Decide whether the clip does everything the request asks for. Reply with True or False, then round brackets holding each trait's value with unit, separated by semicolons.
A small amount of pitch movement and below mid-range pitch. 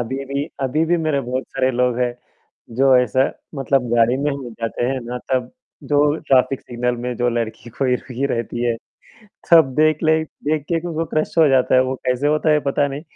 False (3.0 semitones; 130 Hz)